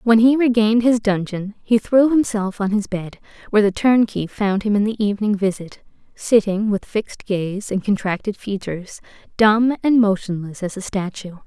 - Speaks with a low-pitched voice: No, high, 210 Hz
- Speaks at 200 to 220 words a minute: No, average, 175 wpm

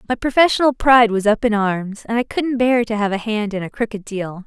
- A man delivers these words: No, female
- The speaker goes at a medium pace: No, fast, 255 wpm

